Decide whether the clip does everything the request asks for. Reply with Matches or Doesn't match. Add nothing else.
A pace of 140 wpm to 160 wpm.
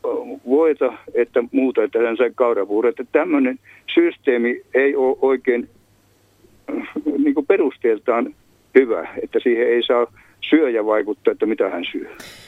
Doesn't match